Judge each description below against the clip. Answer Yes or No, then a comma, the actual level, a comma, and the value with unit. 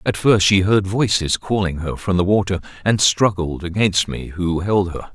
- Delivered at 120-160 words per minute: No, average, 200 wpm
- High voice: No, very low, 95 Hz